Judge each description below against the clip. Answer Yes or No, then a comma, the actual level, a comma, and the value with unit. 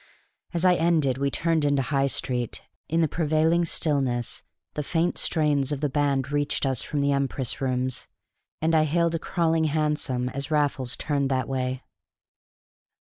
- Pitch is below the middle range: No, medium, 145 Hz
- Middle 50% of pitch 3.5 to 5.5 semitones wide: No, average, 3.1 semitones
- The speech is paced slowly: No, average, 160 wpm